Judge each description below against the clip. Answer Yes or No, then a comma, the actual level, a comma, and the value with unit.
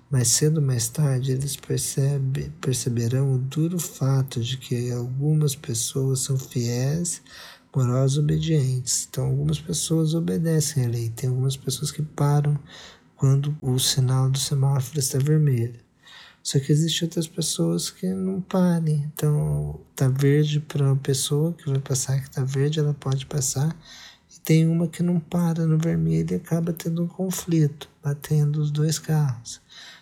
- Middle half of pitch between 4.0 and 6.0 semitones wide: No, average, 3.2 semitones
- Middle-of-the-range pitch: Yes, medium, 145 Hz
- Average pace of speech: Yes, average, 150 wpm